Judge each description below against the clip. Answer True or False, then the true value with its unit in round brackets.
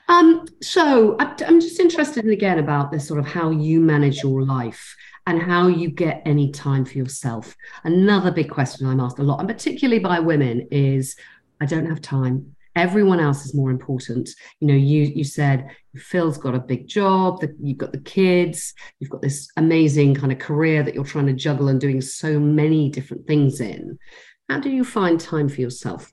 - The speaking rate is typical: True (195 wpm)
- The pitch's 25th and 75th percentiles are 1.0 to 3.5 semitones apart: False (4.4 semitones)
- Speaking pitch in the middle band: True (150 Hz)